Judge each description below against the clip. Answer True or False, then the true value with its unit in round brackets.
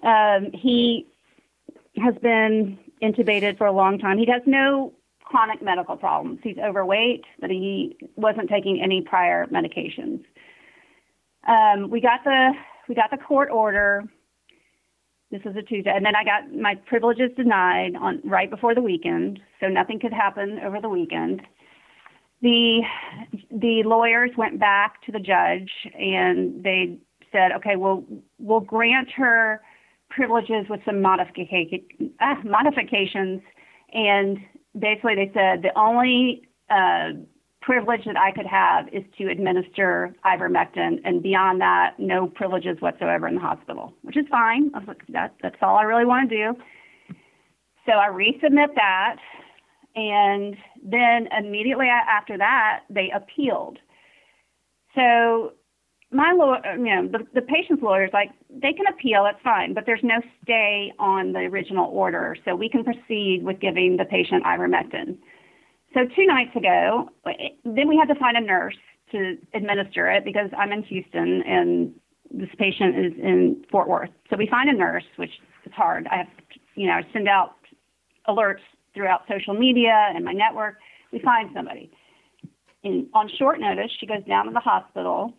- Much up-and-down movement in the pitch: False (3.9 semitones)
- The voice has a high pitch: True (215 Hz)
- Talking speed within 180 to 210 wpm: False (155 wpm)